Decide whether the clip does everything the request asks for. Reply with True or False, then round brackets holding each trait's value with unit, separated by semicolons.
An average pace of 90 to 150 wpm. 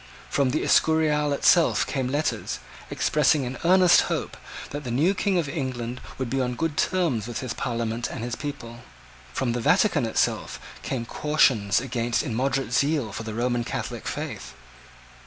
False (160 wpm)